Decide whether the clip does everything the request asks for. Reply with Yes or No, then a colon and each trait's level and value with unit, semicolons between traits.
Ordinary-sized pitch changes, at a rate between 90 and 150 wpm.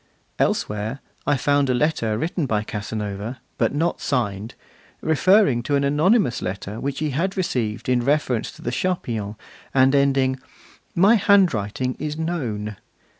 No: wide, 5.9 semitones; average, 140 wpm